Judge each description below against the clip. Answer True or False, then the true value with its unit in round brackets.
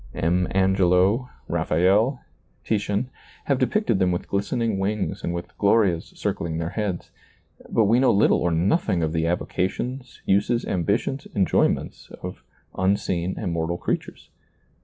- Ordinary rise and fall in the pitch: True (4.3 semitones)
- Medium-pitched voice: False (95 Hz)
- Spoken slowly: True (130 wpm)